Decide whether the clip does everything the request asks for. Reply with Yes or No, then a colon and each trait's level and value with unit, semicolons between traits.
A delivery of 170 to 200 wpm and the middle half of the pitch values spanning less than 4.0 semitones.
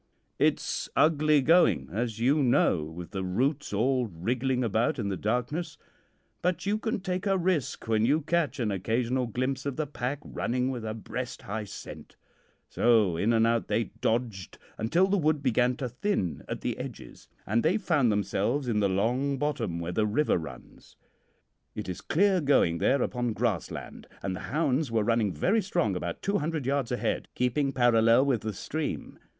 No: average, 180 wpm; average, 5.3 semitones